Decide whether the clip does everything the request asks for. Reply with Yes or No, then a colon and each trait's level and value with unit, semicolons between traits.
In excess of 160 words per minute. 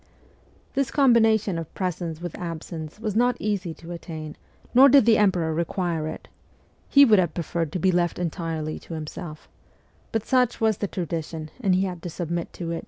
Yes: average, 180 wpm